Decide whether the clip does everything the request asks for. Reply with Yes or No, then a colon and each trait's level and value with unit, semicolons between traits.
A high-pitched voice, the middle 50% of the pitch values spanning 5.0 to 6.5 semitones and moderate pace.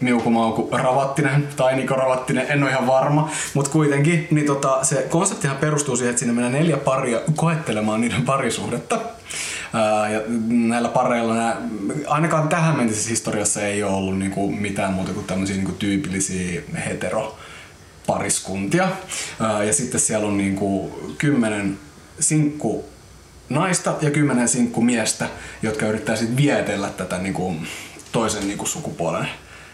No: low, 120 Hz; wide, 5.6 semitones; average, 135 wpm